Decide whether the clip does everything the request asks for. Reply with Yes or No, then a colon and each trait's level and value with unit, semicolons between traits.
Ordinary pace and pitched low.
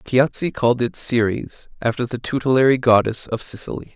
Yes: average, 150 wpm; low, 120 Hz